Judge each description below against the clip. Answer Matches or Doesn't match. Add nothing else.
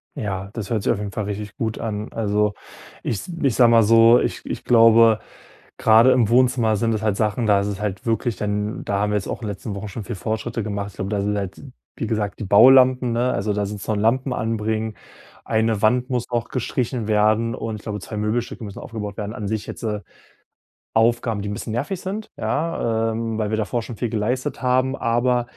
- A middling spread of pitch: Doesn't match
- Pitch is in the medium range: Doesn't match